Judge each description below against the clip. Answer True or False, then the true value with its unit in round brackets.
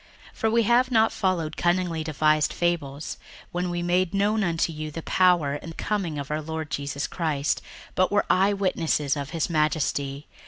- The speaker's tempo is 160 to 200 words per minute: True (170 wpm)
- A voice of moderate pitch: True (165 Hz)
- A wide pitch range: False (3.4 semitones)